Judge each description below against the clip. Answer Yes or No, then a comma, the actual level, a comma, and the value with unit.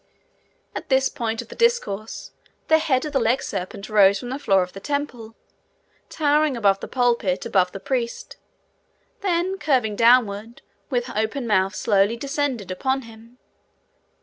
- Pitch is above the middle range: Yes, high, 235 Hz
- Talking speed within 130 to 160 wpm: Yes, average, 150 wpm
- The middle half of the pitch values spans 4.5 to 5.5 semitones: Yes, average, 5.2 semitones